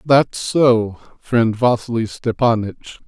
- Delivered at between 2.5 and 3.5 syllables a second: Yes, 3.3 syllables/s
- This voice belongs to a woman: No, male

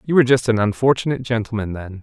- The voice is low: Yes, low, 115 Hz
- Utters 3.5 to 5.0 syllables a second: No, 7.3 syllables/s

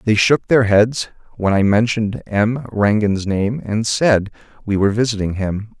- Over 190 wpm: No, average, 165 wpm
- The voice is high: No, low, 110 Hz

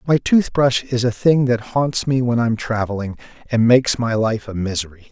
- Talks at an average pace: No, fast, 210 wpm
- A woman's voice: No, male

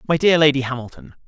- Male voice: Yes, male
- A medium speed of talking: Yes, average, 190 wpm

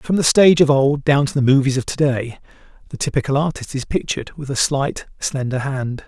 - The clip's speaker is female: No, male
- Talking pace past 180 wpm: Yes, fast, 205 wpm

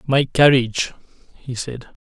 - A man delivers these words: Yes, male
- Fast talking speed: No, slow, 120 wpm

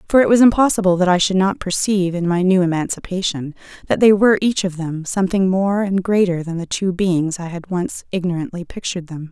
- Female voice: Yes, female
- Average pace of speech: No, fast, 210 wpm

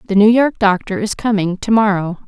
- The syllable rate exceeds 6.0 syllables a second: No, 5.4 syllables/s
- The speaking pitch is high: Yes, high, 205 Hz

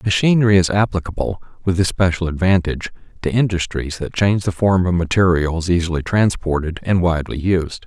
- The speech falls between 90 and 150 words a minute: Yes, average, 145 wpm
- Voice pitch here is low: Yes, very low, 90 Hz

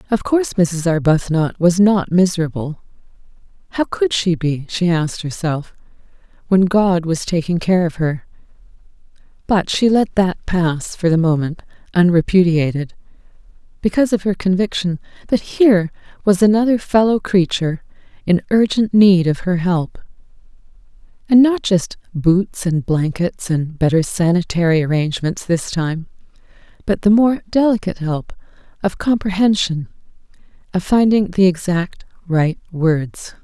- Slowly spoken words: Yes, slow, 125 wpm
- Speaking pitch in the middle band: Yes, medium, 180 Hz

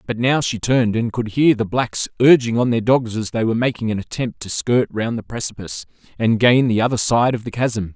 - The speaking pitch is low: Yes, low, 115 Hz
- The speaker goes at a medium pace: No, fast, 240 wpm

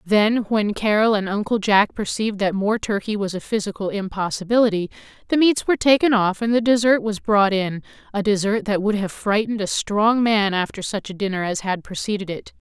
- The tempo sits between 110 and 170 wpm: No, average, 195 wpm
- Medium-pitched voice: No, high, 205 Hz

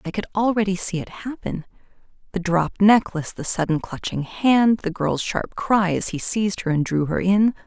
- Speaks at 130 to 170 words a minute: No, average, 190 wpm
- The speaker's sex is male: No, female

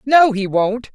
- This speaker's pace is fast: No, average, 190 wpm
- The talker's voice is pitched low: No, high, 230 Hz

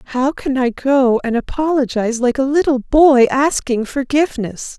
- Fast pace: No, average, 150 wpm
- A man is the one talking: No, female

